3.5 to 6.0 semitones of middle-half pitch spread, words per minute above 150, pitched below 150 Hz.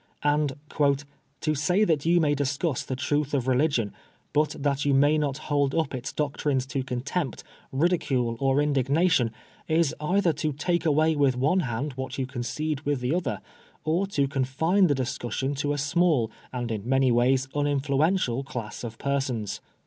No: average, 2.8 semitones; average, 170 wpm; medium, 140 Hz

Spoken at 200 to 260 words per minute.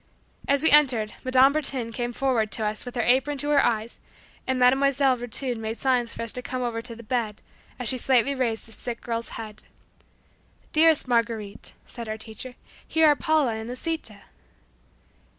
No: average, 175 wpm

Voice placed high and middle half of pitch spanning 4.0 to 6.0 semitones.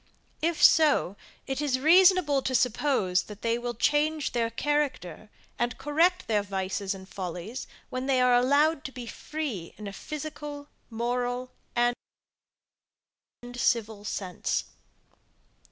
Yes: very high, 250 Hz; wide, 5.6 semitones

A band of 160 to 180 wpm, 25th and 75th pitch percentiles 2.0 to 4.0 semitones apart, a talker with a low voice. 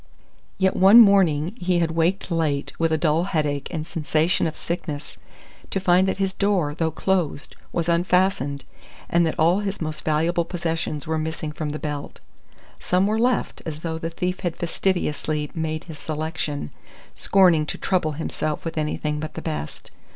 No: average, 170 wpm; average, 2.9 semitones; medium, 165 Hz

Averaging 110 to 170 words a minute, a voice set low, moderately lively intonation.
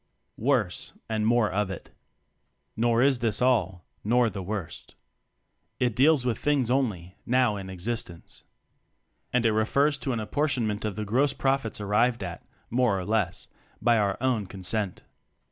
Yes: average, 160 wpm; low, 110 Hz; average, 3.7 semitones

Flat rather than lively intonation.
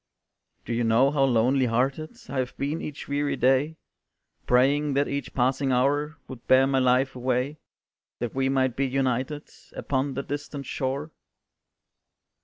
Yes: narrow, 1.8 semitones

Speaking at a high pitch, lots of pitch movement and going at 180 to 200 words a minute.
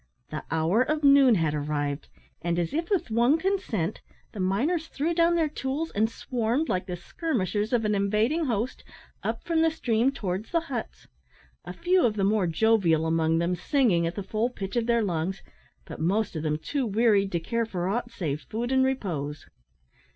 Yes: high, 220 Hz; wide, 7.2 semitones; average, 190 wpm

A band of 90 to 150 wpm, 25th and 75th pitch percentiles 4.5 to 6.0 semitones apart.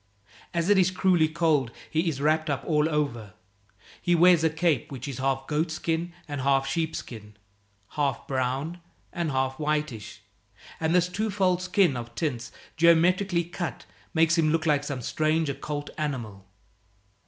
No: average, 145 wpm; average, 3.9 semitones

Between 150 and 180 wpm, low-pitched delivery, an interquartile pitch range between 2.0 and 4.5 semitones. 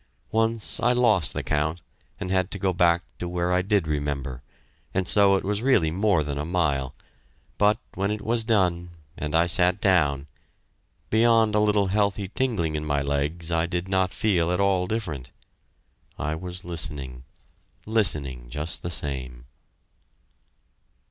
No: average, 155 wpm; very low, 90 Hz; average, 5.1 semitones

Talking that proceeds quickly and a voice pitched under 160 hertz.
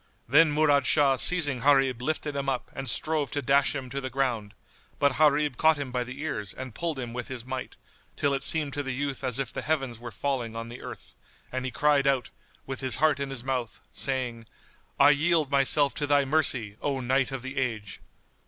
Yes: fast, 215 wpm; low, 135 Hz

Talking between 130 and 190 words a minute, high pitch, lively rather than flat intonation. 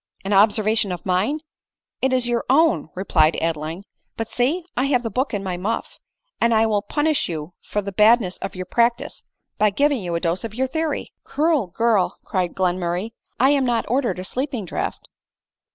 No: average, 200 wpm; high, 220 Hz; wide, 5.7 semitones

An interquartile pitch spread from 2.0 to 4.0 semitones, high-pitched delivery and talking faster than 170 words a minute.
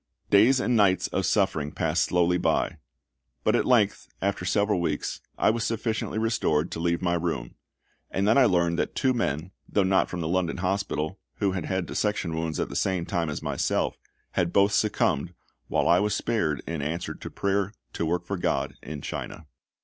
No: average, 3.5 semitones; very low, 90 Hz; average, 190 wpm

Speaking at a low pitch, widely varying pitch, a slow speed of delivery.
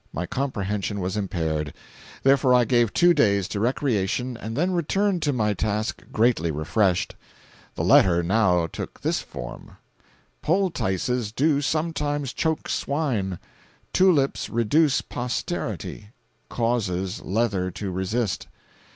Yes: low, 115 Hz; wide, 6.7 semitones; slow, 115 wpm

